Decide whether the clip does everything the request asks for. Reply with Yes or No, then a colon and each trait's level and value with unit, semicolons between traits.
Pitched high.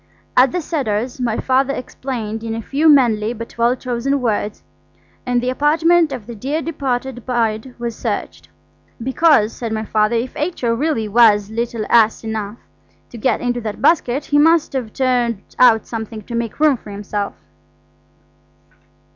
Yes: high, 240 Hz